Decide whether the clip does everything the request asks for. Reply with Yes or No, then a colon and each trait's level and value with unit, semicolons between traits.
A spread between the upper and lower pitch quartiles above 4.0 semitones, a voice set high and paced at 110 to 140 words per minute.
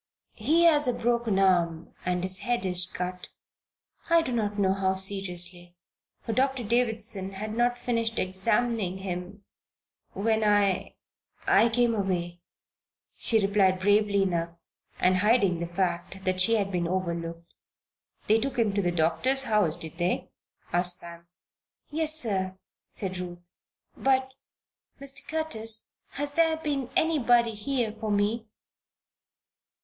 Yes: average, 4.5 semitones; high, 205 Hz; slow, 135 wpm